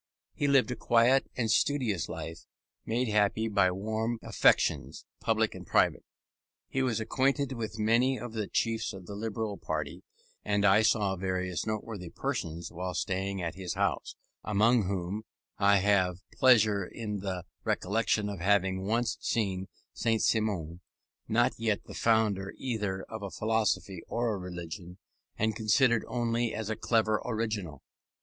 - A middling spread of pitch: Yes, average, 3.2 semitones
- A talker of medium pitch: No, low, 105 Hz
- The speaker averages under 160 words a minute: Yes, average, 150 wpm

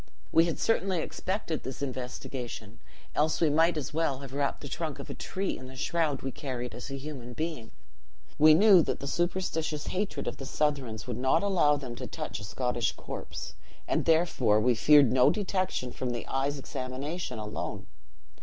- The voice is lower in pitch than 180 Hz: Yes, medium, 140 Hz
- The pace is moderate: Yes, average, 180 wpm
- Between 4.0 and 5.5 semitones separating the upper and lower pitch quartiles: Yes, average, 4.4 semitones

